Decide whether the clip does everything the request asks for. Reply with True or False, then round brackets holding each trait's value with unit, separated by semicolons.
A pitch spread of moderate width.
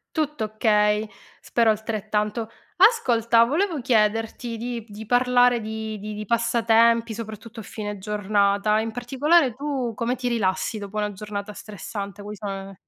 False (2.2 semitones)